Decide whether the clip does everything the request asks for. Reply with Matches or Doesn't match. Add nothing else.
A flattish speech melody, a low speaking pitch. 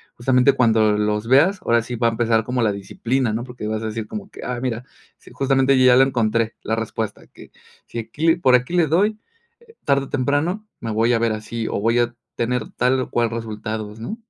Doesn't match